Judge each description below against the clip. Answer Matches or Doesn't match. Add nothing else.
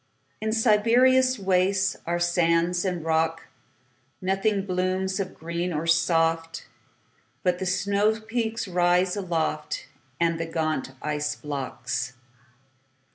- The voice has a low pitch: Doesn't match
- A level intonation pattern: Doesn't match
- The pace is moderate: Doesn't match